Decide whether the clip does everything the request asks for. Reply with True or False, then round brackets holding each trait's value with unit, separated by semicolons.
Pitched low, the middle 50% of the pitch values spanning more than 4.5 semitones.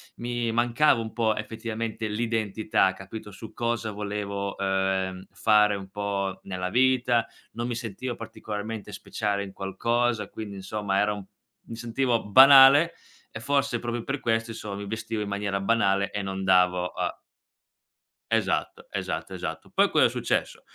False (110 Hz; 2.9 semitones)